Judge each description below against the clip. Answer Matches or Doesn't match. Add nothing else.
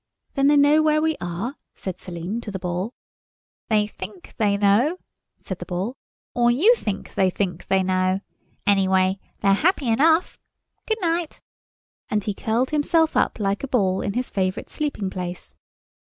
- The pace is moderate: Matches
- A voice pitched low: Doesn't match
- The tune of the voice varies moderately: Doesn't match